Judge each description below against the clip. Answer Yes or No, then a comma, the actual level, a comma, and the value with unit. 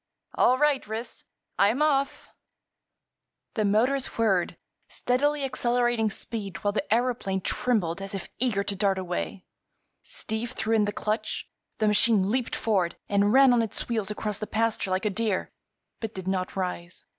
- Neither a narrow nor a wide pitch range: Yes, average, 3.6 semitones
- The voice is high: Yes, high, 215 Hz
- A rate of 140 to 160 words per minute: Yes, average, 155 wpm